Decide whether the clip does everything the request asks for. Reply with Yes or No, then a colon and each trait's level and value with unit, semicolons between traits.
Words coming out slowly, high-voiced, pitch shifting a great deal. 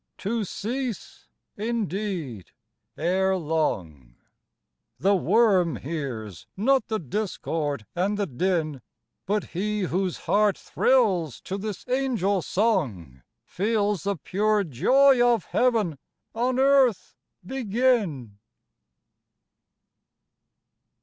Yes: slow, 90 wpm; high, 195 Hz; wide, 5.9 semitones